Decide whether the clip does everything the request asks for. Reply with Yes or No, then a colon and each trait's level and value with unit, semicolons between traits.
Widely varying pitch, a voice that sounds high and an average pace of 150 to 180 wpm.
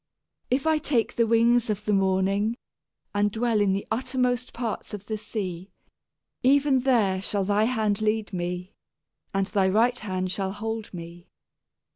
No: average, 3.6 semitones; high, 210 Hz; average, 155 wpm